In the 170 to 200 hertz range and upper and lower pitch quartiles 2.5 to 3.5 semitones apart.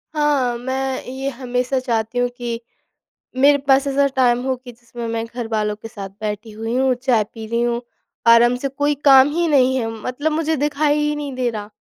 No: very high, 250 Hz; average, 3.0 semitones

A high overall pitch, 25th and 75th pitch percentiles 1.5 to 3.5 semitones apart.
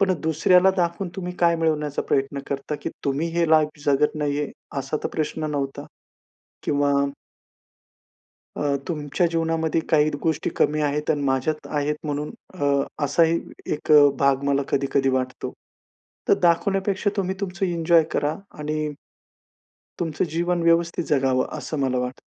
No: medium, 150 Hz; average, 2.9 semitones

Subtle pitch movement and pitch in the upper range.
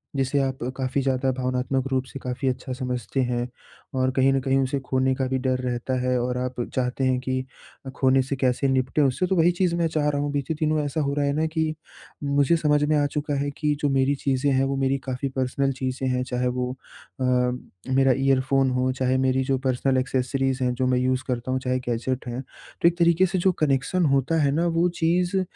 No: narrow, 1.9 semitones; low, 130 Hz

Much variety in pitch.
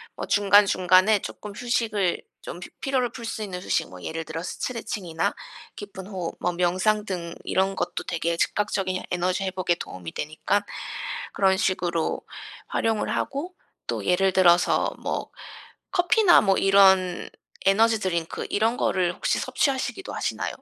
No: average, 3.1 semitones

